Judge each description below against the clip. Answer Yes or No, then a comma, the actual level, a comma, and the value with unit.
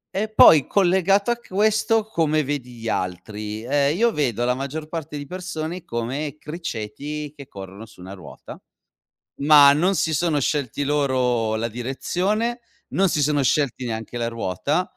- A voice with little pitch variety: No, wide, 6.5 semitones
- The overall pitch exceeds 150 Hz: No, medium, 145 Hz